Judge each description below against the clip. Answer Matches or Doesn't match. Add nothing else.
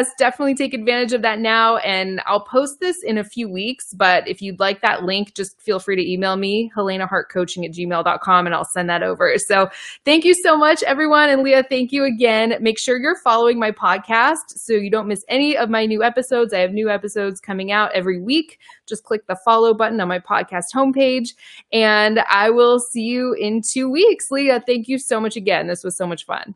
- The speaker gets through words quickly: Matches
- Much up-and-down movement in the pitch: Doesn't match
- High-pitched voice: Matches